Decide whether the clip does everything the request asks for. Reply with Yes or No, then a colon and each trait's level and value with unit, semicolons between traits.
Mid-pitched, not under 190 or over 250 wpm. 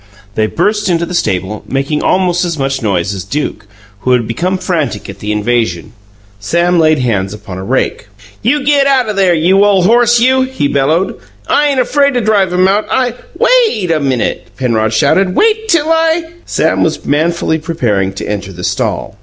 Yes: medium, 170 Hz; average, 195 wpm